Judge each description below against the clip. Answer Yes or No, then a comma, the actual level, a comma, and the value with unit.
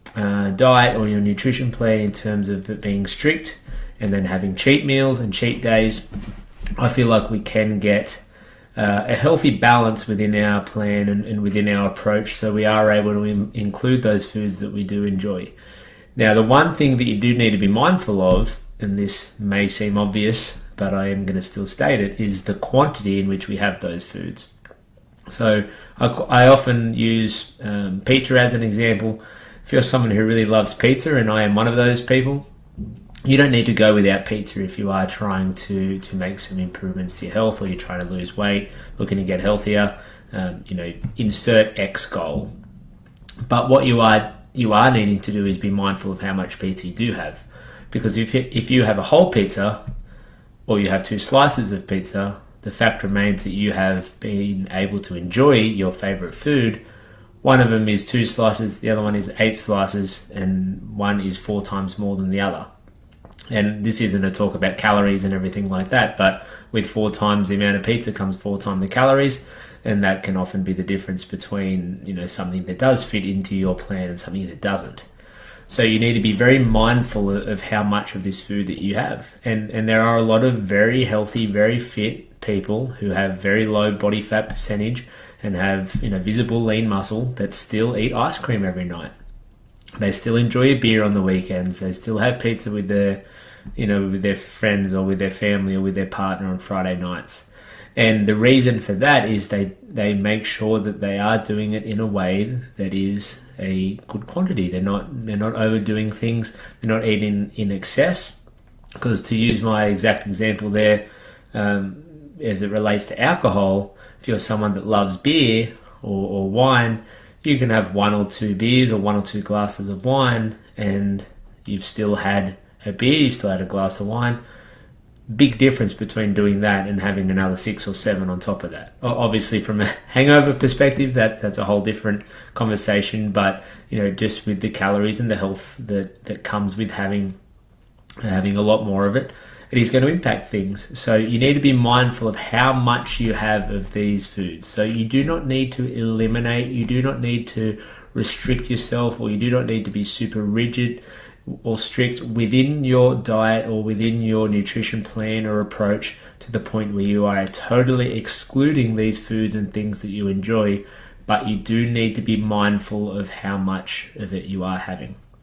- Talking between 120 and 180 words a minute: No, average, 200 wpm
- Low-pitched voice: Yes, low, 105 Hz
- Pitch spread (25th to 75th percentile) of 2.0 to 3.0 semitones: Yes, narrow, 2.4 semitones